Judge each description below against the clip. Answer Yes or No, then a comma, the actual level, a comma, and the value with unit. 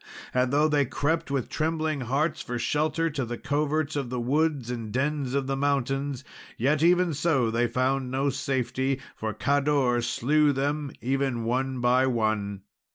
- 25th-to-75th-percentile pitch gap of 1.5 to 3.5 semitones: Yes, average, 3.2 semitones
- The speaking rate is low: No, average, 160 wpm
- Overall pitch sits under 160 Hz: Yes, low, 135 Hz